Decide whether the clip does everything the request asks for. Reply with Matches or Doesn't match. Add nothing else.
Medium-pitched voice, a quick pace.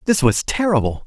Doesn't match